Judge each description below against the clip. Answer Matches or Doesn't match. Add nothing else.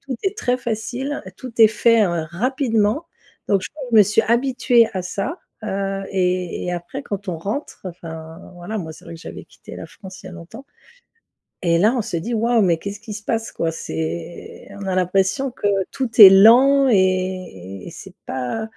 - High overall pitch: Matches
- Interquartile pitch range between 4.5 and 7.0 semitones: Matches